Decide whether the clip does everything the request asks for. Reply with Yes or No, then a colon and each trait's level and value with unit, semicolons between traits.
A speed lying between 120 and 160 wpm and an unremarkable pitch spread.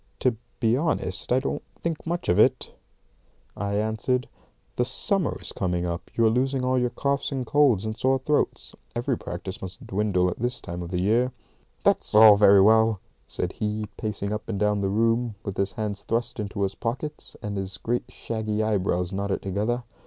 No: average, 185 wpm; average, 3.8 semitones